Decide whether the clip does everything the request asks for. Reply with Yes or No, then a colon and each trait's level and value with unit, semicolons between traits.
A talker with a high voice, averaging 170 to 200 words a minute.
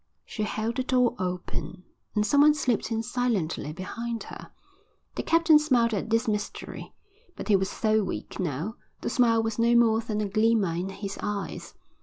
Yes: high, 220 Hz; average, 180 wpm